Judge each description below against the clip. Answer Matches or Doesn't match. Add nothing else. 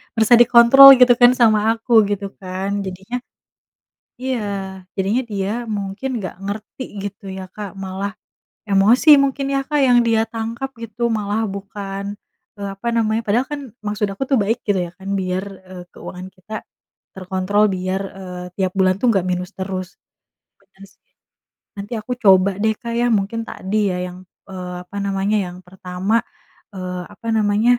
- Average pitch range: Matches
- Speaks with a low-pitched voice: Doesn't match